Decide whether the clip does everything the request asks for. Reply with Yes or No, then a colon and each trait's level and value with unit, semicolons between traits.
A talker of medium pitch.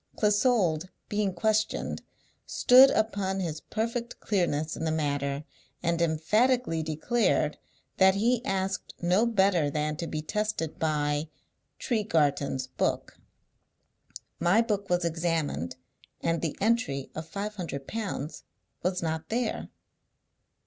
Yes: medium, 175 Hz